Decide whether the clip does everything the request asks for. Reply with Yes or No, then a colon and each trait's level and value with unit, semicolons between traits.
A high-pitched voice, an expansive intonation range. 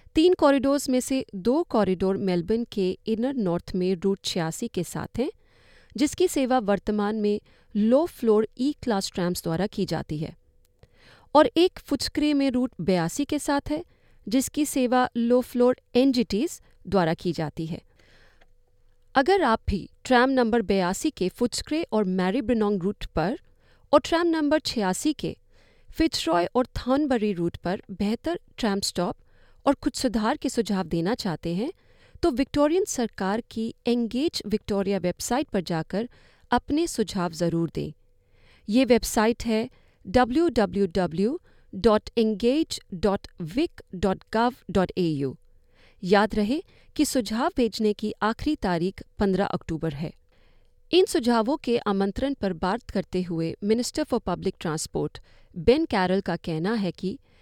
Yes: high, 215 Hz; wide, 6.1 semitones